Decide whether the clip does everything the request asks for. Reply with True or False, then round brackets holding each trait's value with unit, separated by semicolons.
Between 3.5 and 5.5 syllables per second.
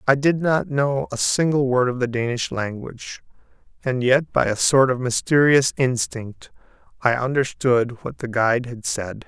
True (4.5 syllables/s)